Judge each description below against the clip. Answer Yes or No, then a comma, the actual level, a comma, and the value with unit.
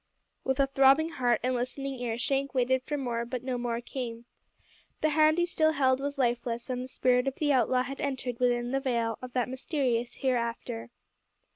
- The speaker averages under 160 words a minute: No, average, 190 wpm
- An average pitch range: No, narrow, 2.1 semitones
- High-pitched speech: Yes, very high, 255 Hz